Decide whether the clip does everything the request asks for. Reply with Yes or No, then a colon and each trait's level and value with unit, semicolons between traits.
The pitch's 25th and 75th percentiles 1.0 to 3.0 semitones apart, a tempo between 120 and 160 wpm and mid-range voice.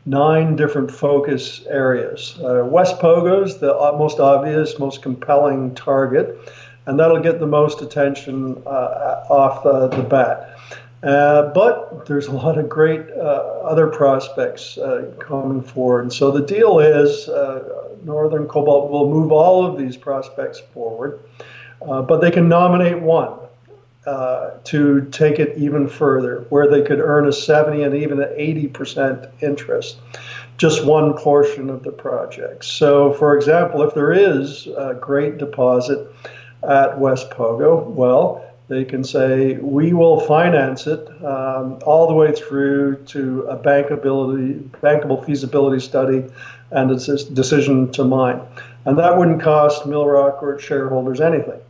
Yes: narrow, 2.4 semitones; average, 150 wpm; medium, 145 Hz